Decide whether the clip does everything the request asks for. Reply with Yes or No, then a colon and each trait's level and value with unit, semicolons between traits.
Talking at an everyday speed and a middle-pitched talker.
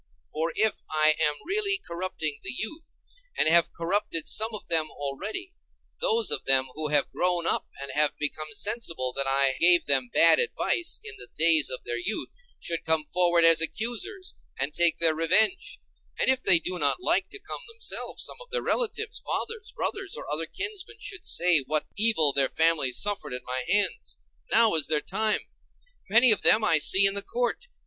Yes: average, 185 wpm; medium, 175 Hz